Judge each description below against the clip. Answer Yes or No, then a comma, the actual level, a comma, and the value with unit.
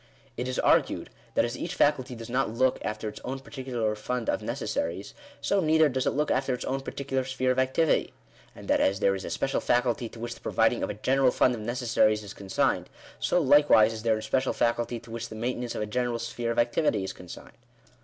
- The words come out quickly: Yes, fast, 225 wpm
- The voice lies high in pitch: No, low, 120 Hz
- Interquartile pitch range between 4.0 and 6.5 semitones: No, average, 2.9 semitones